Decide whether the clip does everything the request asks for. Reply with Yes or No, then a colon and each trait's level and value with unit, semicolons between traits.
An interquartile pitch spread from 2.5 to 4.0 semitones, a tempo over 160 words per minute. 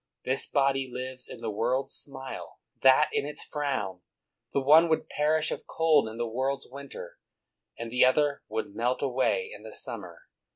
Yes: average, 2.8 semitones; average, 170 wpm